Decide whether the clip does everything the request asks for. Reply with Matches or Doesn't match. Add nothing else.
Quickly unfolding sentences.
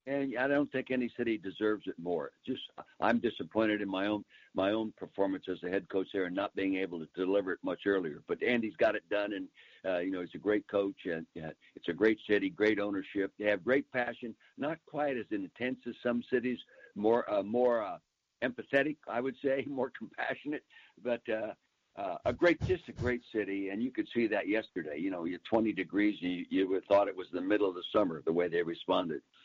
Matches